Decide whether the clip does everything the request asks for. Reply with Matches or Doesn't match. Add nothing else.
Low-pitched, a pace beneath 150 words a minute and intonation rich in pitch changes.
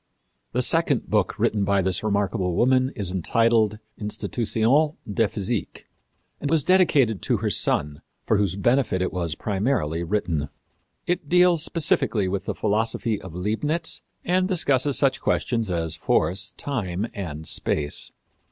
Matches